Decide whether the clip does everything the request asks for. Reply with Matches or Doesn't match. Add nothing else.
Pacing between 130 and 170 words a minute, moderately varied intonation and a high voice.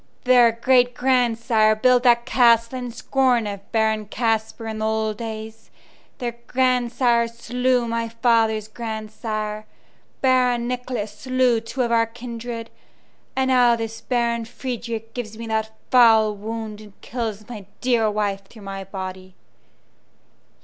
Doesn't match